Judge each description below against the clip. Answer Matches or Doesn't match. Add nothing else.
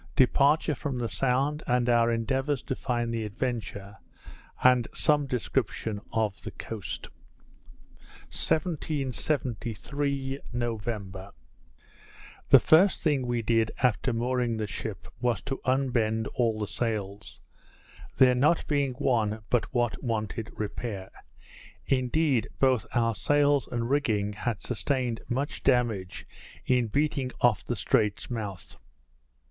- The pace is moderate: Doesn't match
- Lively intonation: Doesn't match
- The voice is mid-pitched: Doesn't match